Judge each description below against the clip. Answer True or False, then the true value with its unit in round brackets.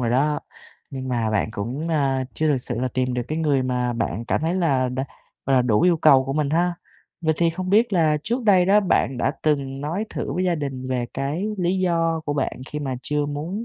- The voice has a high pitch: False (145 Hz)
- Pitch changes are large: False (4.6 semitones)